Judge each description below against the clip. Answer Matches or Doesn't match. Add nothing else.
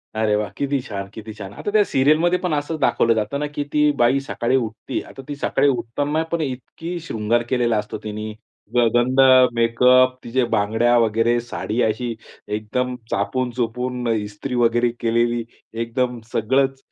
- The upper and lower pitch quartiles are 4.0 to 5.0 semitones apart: Doesn't match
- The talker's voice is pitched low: Matches